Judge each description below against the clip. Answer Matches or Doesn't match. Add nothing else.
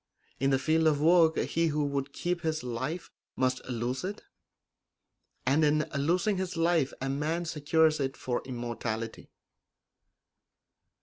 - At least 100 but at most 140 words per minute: Matches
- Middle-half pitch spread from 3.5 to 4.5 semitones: Matches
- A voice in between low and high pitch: Matches